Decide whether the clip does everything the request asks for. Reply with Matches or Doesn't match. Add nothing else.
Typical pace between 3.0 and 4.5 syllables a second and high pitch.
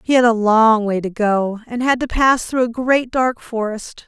Matches